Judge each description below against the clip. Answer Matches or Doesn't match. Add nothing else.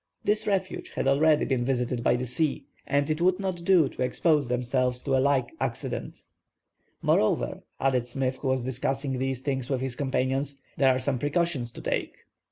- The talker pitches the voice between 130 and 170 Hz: Matches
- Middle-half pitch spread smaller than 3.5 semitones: Matches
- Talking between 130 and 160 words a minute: Doesn't match